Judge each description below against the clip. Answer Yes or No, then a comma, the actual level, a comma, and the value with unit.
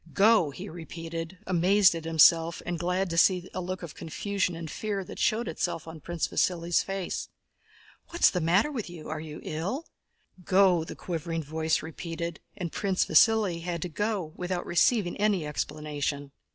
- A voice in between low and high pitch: Yes, medium, 175 Hz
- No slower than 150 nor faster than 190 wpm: Yes, average, 165 wpm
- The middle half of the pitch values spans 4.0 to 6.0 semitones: No, average, 2.9 semitones